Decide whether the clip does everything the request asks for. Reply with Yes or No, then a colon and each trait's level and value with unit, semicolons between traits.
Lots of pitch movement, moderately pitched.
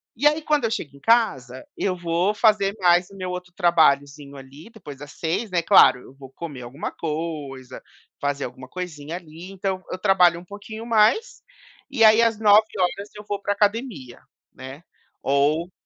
Yes: wide, 6.3 semitones; medium, 180 Hz